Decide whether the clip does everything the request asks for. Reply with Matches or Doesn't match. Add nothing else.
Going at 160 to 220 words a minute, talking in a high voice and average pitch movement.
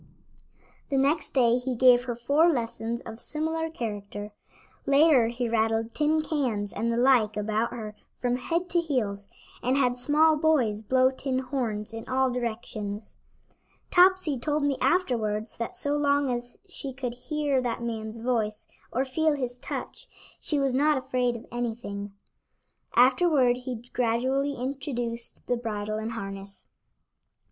Doesn't match